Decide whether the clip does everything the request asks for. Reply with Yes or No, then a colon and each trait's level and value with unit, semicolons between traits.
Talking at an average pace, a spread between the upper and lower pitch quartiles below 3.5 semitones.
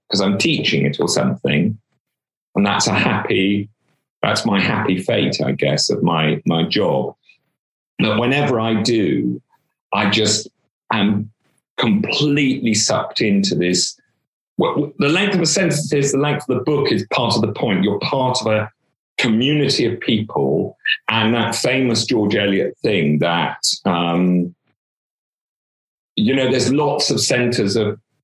No: average, 145 wpm; wide, 5.6 semitones